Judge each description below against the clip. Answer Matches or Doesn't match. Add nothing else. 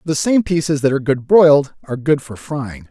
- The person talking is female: Doesn't match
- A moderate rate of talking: Doesn't match